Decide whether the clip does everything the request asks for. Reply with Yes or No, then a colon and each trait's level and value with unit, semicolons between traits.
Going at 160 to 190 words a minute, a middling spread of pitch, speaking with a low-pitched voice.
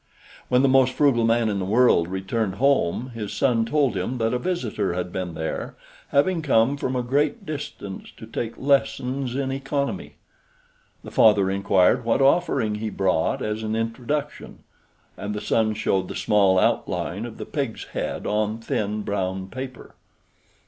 Yes: average, 165 wpm; average, 4.7 semitones; low, 115 Hz